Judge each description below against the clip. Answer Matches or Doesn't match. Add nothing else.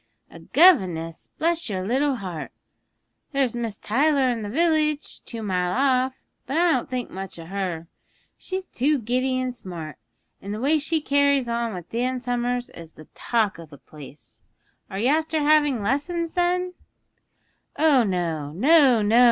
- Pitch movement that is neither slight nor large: Doesn't match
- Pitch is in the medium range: Doesn't match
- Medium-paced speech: Matches